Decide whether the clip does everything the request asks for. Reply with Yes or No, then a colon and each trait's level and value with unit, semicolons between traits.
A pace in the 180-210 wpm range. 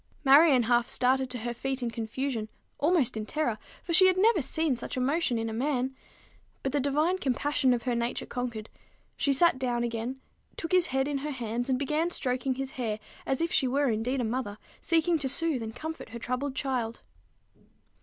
Yes: average, 195 wpm